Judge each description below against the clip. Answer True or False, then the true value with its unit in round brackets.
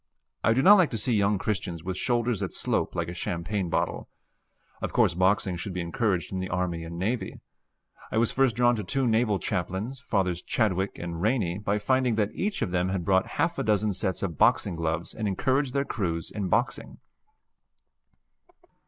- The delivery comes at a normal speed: True (190 wpm)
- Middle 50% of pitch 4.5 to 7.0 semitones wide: True (4.8 semitones)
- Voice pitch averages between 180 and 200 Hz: False (100 Hz)